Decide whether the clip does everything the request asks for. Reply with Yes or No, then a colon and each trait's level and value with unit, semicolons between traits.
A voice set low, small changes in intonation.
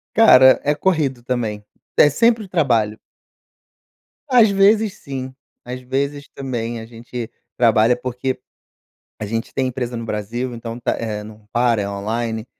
No: low, 125 Hz; average, 3.5 semitones